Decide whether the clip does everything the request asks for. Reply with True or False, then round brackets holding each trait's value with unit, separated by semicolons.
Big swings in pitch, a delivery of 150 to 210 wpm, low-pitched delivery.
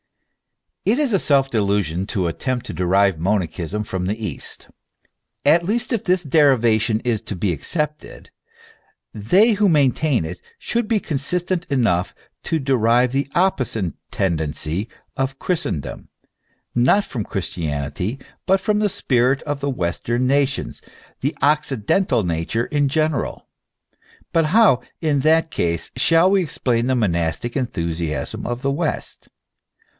False (8.0 semitones; 135 wpm; 125 Hz)